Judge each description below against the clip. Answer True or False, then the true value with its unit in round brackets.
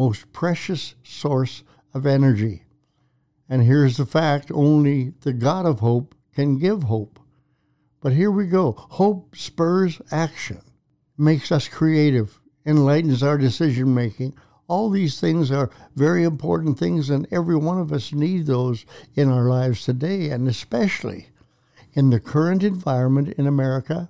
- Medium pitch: True (145 Hz)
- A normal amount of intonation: True (3.5 semitones)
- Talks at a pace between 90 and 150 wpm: True (140 wpm)